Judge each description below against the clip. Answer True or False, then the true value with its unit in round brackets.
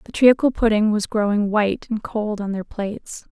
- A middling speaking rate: True (195 wpm)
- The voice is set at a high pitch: True (215 Hz)